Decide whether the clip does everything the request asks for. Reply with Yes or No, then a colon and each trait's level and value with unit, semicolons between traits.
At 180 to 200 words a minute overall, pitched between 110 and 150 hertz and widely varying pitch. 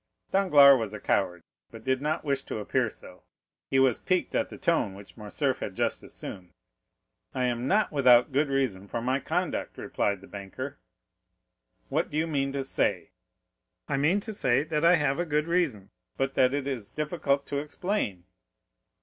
No: average, 185 wpm; low, 135 Hz; average, 4.3 semitones